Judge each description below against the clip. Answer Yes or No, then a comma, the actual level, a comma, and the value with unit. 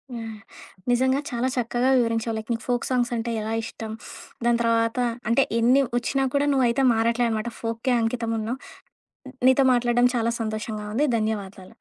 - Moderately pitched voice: No, high, 235 Hz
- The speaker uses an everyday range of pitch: No, narrow, 1.6 semitones